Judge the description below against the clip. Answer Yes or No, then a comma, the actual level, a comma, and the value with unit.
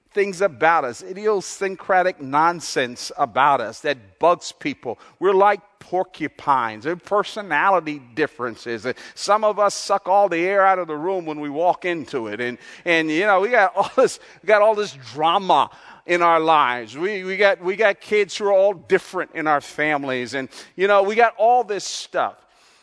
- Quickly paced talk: No, average, 185 wpm